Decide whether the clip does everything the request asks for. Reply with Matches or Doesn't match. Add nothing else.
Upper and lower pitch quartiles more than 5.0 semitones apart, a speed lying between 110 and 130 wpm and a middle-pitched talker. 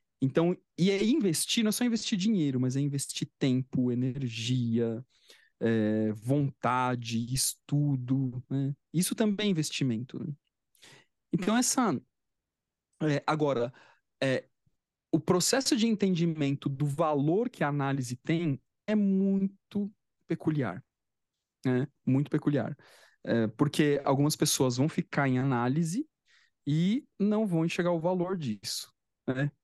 Matches